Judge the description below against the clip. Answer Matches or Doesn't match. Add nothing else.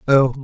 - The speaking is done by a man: Matches